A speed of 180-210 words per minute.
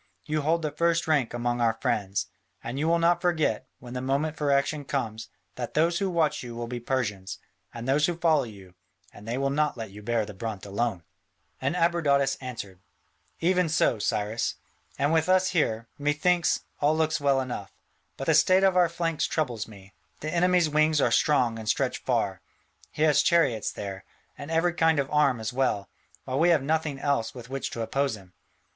Yes: average, 195 wpm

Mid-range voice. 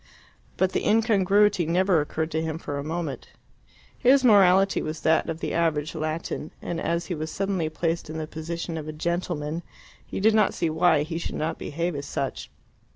Yes: medium, 165 Hz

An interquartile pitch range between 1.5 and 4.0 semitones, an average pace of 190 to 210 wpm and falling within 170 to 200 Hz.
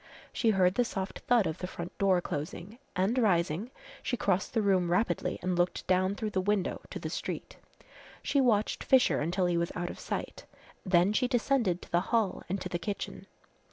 Yes: average, 3.7 semitones; average, 195 wpm; high, 190 Hz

